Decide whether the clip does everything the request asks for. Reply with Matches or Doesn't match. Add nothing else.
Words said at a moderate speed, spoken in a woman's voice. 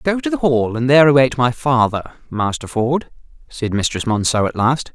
Doesn't match